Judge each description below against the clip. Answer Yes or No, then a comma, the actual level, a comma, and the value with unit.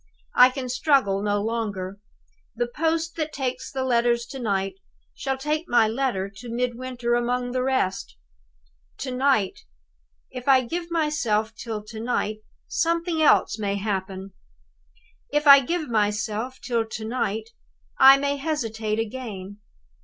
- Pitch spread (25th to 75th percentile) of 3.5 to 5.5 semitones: Yes, average, 4.1 semitones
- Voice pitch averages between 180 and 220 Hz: No, high, 240 Hz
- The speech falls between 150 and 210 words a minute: No, average, 140 wpm